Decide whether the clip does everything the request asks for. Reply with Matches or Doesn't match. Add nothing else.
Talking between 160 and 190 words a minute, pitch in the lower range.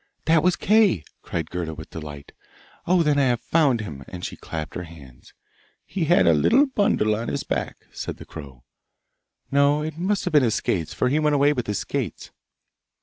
Doesn't match